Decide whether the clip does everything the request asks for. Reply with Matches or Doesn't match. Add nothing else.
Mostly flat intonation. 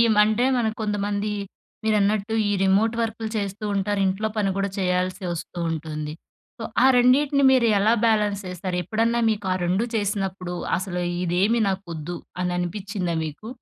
Doesn't match